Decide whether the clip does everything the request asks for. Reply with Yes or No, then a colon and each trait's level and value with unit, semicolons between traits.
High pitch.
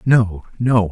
No: low, 110 Hz